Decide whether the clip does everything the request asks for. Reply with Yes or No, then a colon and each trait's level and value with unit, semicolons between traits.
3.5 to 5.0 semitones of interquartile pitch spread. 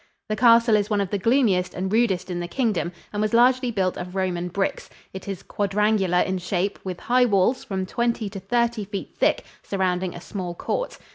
Yes: average, 3.8 semitones